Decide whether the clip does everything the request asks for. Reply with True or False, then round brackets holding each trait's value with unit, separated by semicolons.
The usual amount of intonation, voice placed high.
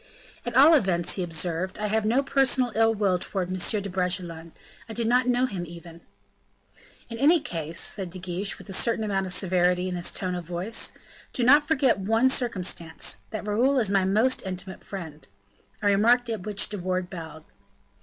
True (4.4 semitones; 195 Hz)